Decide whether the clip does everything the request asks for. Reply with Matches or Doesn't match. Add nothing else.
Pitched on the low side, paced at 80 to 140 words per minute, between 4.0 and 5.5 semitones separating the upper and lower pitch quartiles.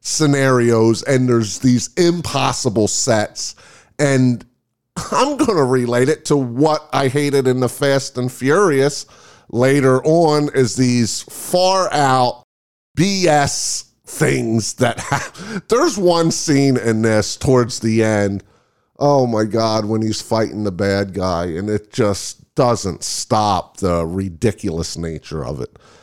Matches